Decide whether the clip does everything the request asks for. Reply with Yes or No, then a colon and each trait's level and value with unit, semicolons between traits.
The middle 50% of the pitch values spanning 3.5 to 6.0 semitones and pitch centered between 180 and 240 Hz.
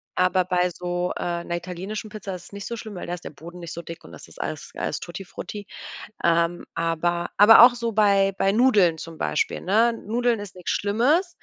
Yes: average, 3.8 semitones; medium, 185 Hz